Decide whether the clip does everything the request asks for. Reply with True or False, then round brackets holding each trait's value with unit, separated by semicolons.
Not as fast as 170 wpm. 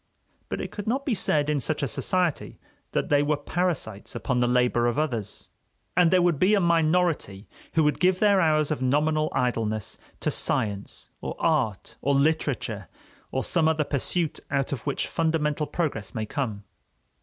False (175 wpm)